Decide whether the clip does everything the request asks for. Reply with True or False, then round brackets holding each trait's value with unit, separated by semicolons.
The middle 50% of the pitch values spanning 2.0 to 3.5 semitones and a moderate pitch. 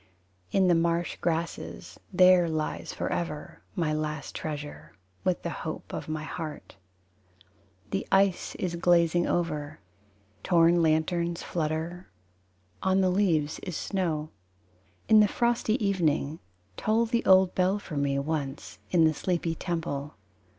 True (2.9 semitones; 170 Hz)